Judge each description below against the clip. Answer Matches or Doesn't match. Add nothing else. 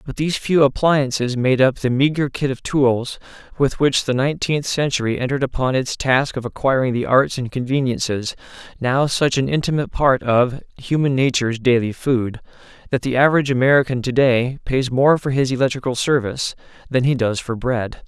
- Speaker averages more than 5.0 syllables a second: Matches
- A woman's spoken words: Doesn't match